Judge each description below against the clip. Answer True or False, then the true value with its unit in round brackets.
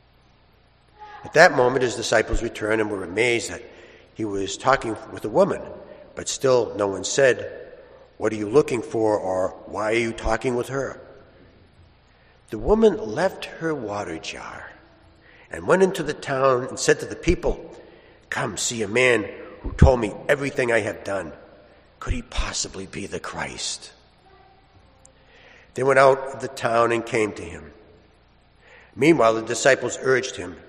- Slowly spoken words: False (160 wpm)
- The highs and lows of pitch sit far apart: True (6.8 semitones)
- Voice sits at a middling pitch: False (125 Hz)